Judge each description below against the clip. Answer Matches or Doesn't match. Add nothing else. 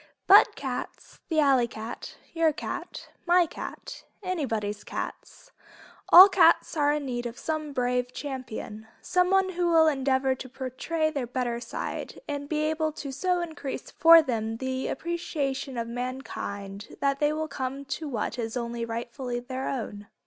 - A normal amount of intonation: Matches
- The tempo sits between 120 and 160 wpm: Matches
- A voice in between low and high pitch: Doesn't match